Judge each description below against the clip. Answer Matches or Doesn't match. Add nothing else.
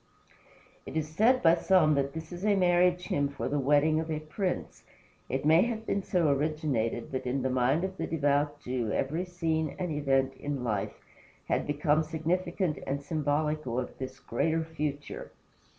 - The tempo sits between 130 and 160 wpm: Doesn't match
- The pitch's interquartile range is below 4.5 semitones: Matches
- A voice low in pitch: Doesn't match